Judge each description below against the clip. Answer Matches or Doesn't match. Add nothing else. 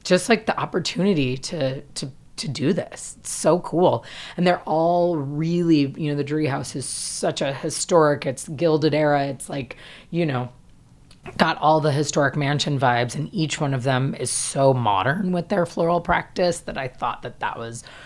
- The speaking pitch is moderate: Matches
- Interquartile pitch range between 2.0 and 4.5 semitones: Matches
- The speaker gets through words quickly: Doesn't match